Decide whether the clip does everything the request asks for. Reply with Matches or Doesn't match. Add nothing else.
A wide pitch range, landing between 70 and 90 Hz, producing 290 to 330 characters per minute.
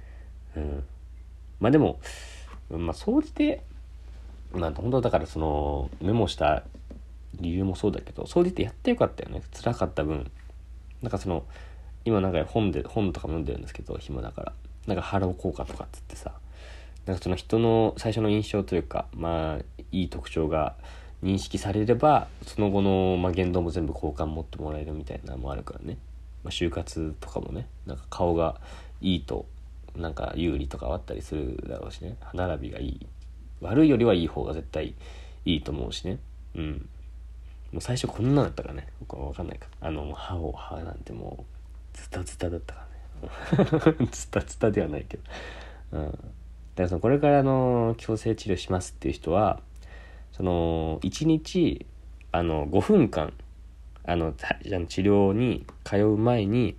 Matches